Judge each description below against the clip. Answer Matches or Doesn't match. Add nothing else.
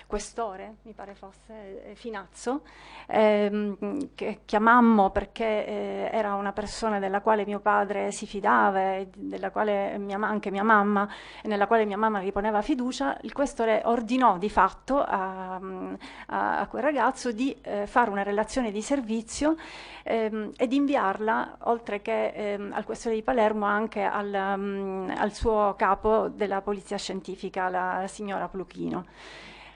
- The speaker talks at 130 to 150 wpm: Matches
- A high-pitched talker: Matches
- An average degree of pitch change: Doesn't match